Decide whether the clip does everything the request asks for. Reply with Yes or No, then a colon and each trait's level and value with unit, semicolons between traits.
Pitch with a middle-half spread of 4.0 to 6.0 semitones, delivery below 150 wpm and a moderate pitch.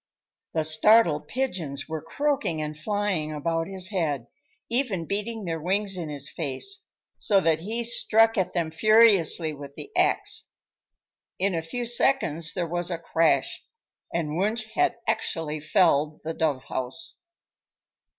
Yes: wide, 5.4 semitones; average, 140 wpm; medium, 170 Hz